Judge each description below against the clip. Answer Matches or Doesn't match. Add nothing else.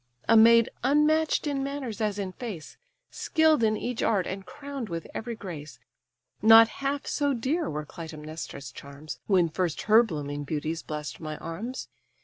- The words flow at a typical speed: Matches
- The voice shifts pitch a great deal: Matches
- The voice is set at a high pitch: Matches